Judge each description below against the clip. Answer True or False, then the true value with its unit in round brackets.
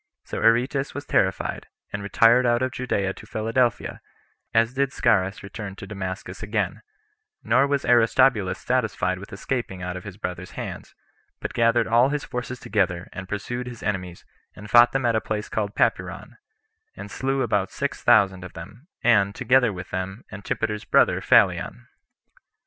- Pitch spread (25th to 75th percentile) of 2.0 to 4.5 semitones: True (4.1 semitones)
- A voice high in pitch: False (110 Hz)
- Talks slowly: False (160 wpm)